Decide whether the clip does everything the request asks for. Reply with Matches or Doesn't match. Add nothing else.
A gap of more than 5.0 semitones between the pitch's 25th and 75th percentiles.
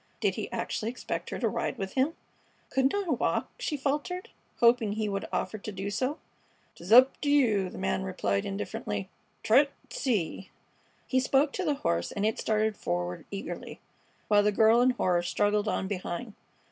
Matches